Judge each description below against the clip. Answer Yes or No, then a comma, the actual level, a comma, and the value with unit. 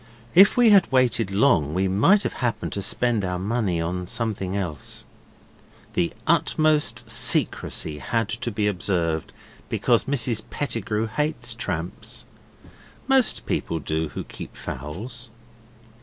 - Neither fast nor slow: No, slow, 125 wpm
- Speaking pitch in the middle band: No, low, 110 Hz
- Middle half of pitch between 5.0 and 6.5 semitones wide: Yes, average, 5.3 semitones